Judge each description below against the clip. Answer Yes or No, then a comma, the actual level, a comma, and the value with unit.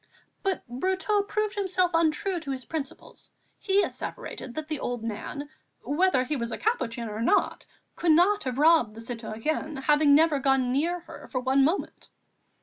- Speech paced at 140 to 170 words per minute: Yes, average, 165 wpm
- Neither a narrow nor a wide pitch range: No, wide, 5.8 semitones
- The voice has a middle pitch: No, very high, 300 Hz